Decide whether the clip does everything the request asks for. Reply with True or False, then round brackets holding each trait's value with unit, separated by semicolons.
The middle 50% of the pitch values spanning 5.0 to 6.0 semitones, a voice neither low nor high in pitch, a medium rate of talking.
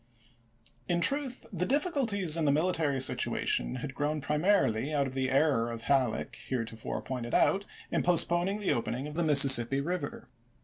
True (5.3 semitones; 150 Hz; 160 wpm)